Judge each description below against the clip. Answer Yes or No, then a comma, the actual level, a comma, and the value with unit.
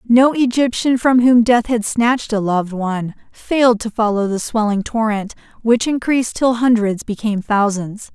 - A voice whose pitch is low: No, high, 225 Hz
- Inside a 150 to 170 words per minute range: Yes, average, 160 wpm